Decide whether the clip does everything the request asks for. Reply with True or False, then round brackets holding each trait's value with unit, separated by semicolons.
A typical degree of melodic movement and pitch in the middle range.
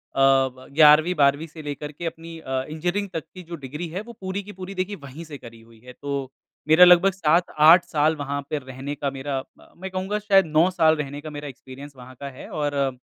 True (4.1 semitones; 150 Hz)